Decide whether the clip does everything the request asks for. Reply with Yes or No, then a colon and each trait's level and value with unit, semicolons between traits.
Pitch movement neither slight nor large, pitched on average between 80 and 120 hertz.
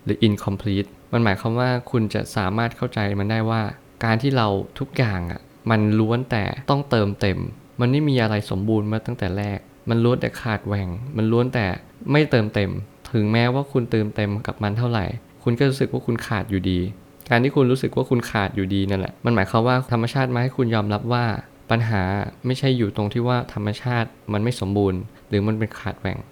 Yes: average, 3.2 semitones; low, 115 Hz